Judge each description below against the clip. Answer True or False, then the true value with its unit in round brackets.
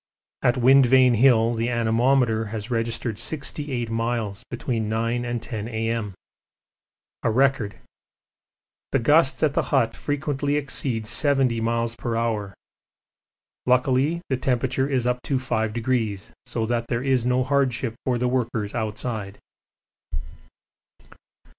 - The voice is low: True (120 Hz)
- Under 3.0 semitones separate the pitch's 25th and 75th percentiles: True (2.5 semitones)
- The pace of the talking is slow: True (120 wpm)